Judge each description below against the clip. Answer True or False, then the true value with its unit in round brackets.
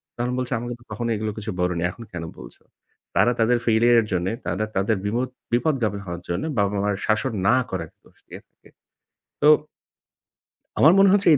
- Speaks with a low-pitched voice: True (110 Hz)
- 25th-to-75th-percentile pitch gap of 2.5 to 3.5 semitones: False (3.9 semitones)